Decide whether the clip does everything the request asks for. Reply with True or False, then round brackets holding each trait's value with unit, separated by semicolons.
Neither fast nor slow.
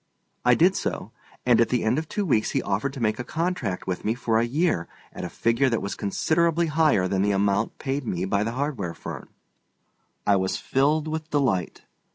False (210 wpm)